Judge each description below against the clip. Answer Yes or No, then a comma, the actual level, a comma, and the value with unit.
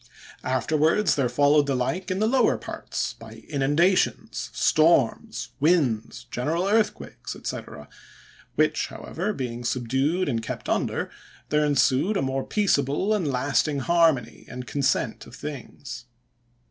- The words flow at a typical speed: No, slow, 125 wpm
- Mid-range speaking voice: Yes, medium, 145 Hz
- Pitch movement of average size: Yes, average, 4.9 semitones